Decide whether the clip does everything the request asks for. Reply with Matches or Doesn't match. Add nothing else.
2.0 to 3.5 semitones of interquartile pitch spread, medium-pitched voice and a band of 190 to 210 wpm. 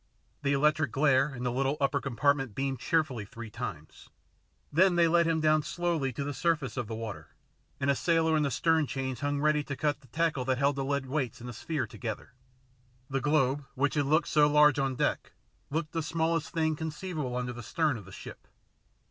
Matches